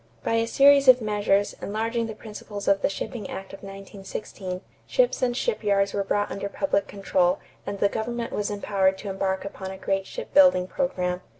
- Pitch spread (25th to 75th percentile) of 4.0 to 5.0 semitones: No, average, 2.8 semitones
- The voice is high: Yes, high, 200 Hz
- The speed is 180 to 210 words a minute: Yes, average, 185 wpm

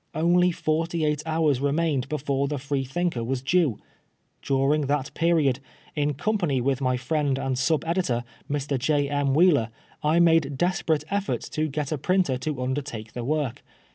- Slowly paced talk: No, average, 160 wpm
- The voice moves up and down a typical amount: Yes, average, 3.3 semitones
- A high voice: No, medium, 145 Hz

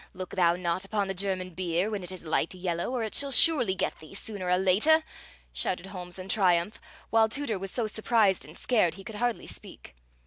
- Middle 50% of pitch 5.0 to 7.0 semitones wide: No, average, 3.4 semitones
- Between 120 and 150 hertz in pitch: No, high, 190 Hz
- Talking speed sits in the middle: No, fast, 210 wpm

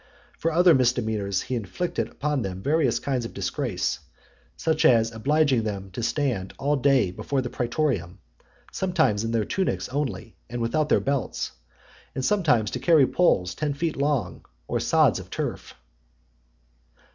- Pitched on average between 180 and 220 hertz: No, low, 125 Hz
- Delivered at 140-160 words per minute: Yes, average, 145 wpm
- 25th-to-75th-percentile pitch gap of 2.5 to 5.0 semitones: No, wide, 5.5 semitones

